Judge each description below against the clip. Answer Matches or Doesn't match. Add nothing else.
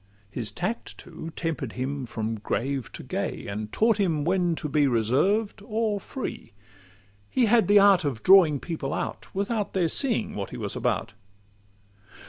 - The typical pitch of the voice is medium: Matches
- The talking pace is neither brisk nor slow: Matches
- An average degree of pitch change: Doesn't match